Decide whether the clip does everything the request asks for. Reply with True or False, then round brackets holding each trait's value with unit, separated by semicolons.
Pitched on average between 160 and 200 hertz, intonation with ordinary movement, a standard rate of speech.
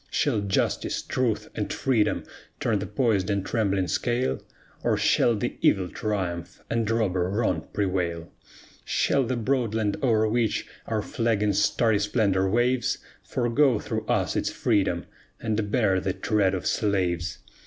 False (105 Hz; 3.4 semitones; 145 wpm)